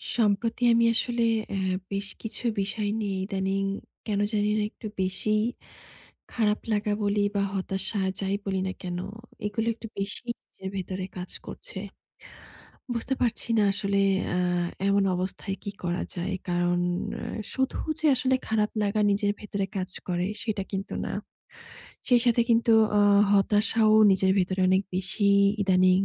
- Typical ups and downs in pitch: No, narrow, 2.2 semitones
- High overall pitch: Yes, high, 200 Hz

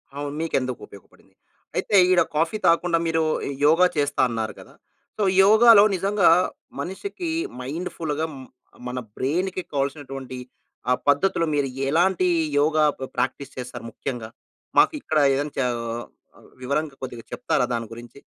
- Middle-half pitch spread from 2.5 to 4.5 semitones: No, average, 5.1 semitones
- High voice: No, medium, 145 Hz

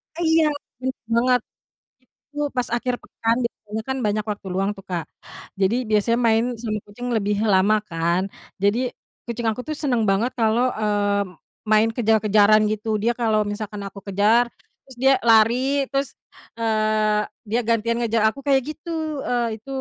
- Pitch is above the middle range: Yes, high, 220 Hz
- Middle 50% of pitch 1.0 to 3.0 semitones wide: Yes, narrow, 2.5 semitones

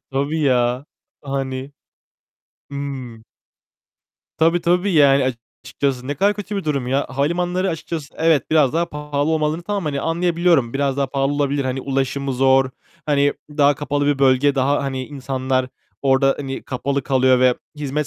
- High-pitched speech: No, medium, 140 Hz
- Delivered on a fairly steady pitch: Yes, narrow, 2.3 semitones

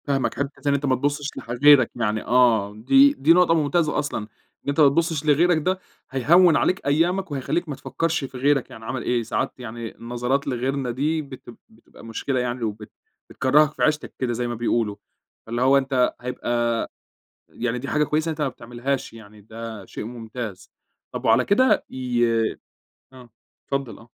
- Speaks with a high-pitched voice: No, low, 130 Hz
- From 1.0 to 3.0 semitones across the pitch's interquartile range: No, average, 3.8 semitones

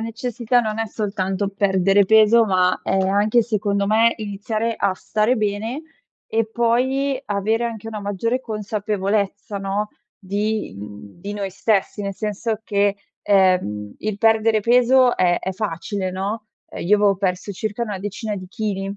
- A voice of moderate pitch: No, high, 210 Hz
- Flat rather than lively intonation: Yes, narrow, 2.3 semitones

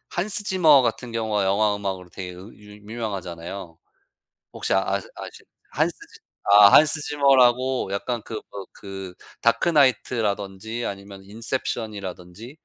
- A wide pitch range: No, average, 4.1 semitones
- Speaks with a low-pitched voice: Yes, low, 105 Hz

